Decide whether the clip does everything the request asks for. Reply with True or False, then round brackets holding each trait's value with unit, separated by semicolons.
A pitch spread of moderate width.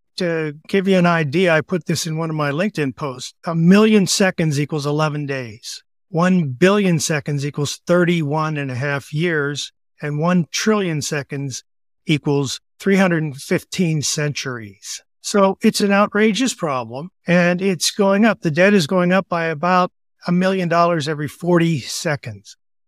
True (4.0 semitones)